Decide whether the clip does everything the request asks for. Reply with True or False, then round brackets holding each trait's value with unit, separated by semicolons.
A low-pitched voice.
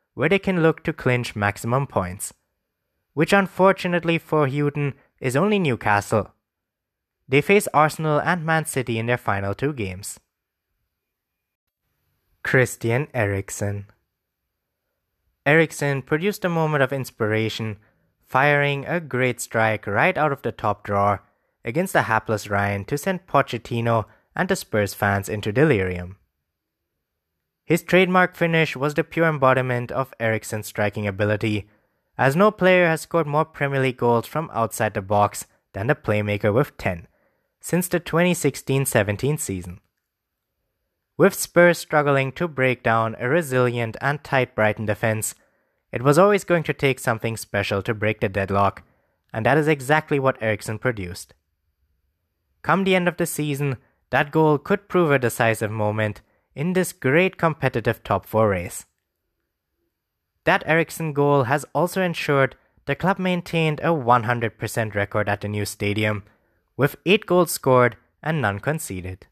True (120 Hz)